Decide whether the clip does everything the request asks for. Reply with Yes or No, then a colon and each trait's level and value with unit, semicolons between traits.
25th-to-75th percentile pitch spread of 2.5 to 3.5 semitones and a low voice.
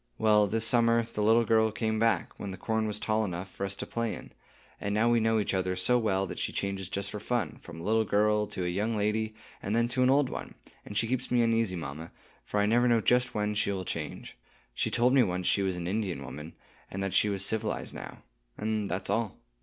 Yes: average, 2.8 semitones; low, 105 Hz